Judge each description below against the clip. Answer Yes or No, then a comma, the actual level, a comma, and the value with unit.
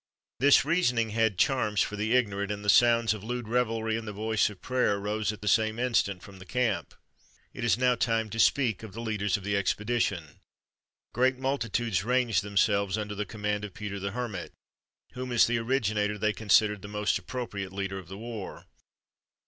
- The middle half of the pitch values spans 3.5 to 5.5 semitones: No, average, 2.7 semitones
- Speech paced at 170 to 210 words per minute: Yes, average, 190 wpm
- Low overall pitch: Yes, low, 110 Hz